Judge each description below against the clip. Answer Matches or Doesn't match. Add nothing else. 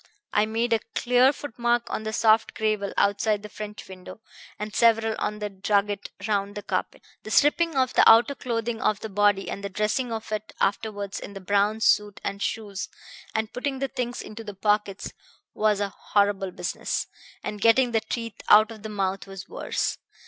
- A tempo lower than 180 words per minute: Doesn't match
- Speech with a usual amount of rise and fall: Doesn't match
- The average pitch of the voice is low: Doesn't match